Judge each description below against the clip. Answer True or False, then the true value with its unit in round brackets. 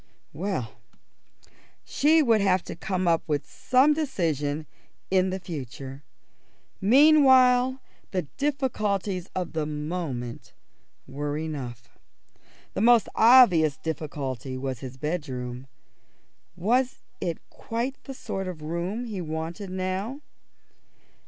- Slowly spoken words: True (105 wpm)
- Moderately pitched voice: True (180 Hz)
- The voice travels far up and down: True (7.5 semitones)